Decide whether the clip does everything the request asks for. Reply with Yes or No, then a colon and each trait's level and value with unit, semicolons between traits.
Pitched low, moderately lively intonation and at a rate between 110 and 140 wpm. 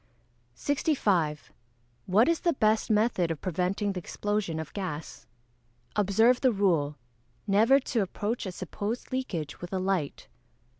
No: high, 200 Hz; average, 4.1 semitones; slow, 135 wpm